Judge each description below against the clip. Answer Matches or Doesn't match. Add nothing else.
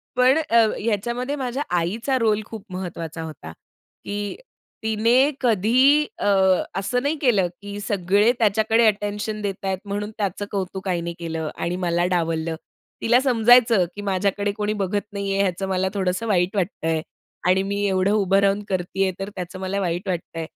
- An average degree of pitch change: Matches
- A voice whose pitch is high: Matches